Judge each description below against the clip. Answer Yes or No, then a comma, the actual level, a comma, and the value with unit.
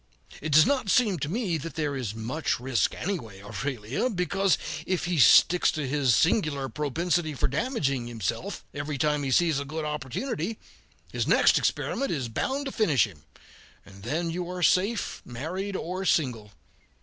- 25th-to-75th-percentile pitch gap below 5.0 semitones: No, wide, 5.6 semitones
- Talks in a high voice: No, medium, 155 Hz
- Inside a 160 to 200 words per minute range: Yes, average, 165 wpm